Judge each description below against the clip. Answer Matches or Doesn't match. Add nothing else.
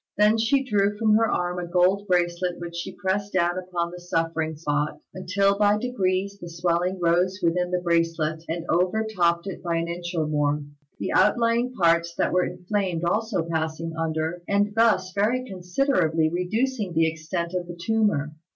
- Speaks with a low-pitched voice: Doesn't match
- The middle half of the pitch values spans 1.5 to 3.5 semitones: Matches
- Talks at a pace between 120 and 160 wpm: Doesn't match